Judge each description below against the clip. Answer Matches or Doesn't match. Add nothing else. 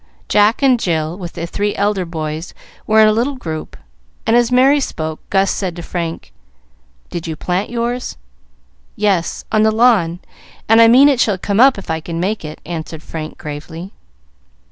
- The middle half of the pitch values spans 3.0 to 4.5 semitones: Doesn't match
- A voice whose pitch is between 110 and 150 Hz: Doesn't match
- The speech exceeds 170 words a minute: Matches